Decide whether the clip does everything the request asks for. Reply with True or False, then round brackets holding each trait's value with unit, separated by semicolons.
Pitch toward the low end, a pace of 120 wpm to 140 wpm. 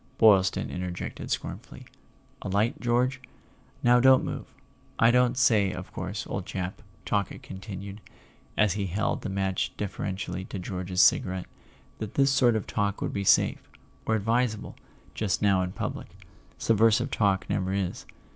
True (100 Hz; 135 wpm)